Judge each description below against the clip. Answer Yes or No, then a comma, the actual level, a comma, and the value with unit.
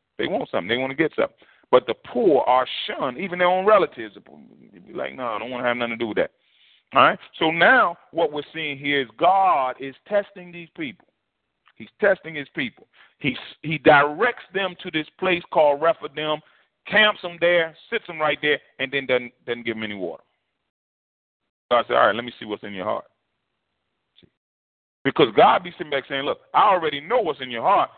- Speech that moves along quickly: Yes, fast, 210 wpm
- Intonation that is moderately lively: No, wide, 5.9 semitones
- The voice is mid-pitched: Yes, medium, 150 Hz